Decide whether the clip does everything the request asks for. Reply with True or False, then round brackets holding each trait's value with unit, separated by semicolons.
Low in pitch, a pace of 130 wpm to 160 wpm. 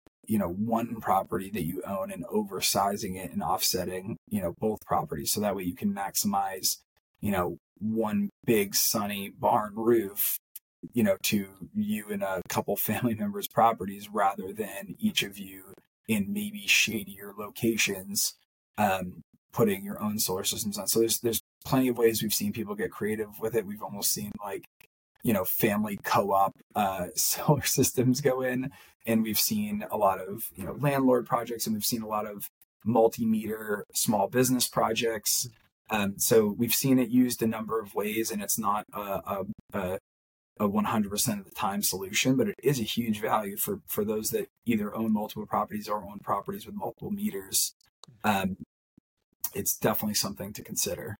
False (115 Hz; 175 wpm)